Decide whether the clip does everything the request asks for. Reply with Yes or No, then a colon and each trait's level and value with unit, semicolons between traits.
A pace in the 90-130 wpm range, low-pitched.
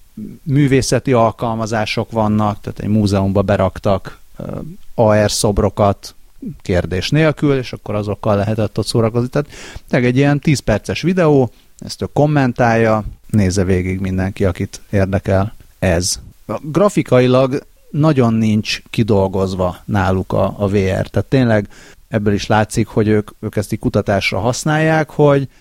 Yes: average, 125 wpm; low, 110 Hz